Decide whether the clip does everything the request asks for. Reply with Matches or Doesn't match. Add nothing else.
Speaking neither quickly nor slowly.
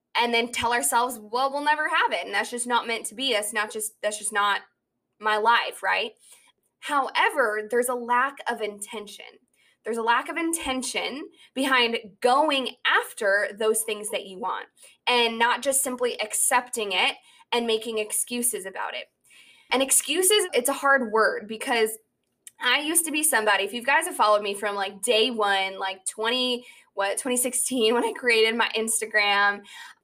Matches